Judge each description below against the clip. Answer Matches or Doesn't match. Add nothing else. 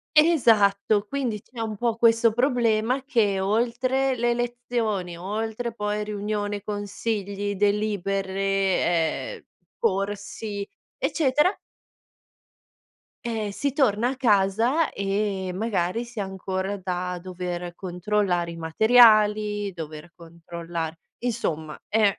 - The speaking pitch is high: Matches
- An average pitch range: Matches